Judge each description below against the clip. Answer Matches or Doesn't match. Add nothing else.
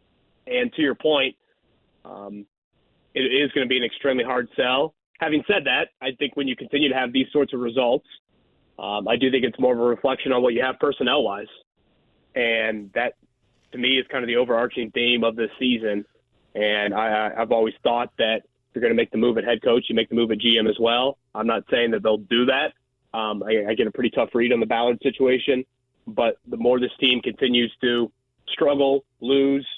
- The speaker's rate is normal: Doesn't match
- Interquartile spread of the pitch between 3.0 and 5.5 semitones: Doesn't match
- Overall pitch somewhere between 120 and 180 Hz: Matches